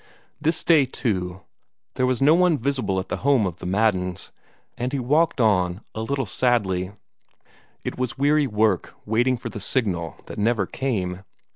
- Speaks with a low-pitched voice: Yes, low, 115 Hz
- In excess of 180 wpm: No, average, 165 wpm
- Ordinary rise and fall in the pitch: No, wide, 6.0 semitones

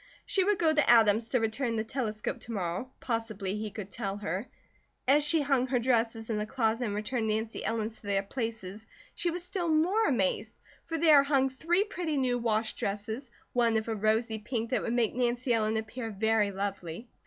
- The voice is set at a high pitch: Yes, high, 230 Hz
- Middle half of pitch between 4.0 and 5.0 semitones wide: No, average, 3.5 semitones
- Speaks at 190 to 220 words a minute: Yes, average, 200 wpm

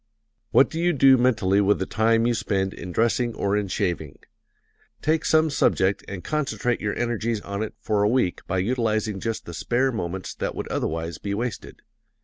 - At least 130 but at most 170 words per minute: No, average, 185 wpm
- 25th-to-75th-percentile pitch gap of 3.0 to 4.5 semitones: Yes, average, 4.1 semitones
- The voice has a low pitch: Yes, low, 110 Hz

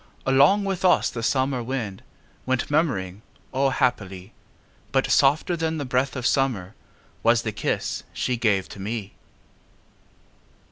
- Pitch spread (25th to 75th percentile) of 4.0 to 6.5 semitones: Yes, average, 4.4 semitones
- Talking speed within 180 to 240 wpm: No, slow, 135 wpm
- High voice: No, low, 130 Hz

